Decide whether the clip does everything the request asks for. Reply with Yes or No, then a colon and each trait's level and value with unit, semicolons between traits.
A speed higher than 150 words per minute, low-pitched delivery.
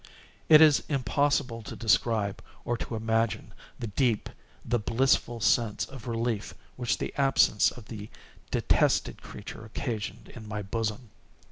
No: slow, 135 wpm; low, 115 Hz